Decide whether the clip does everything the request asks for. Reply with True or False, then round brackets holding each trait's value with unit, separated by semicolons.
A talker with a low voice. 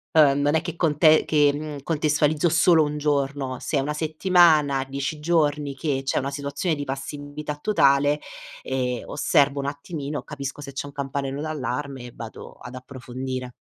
False (145 Hz)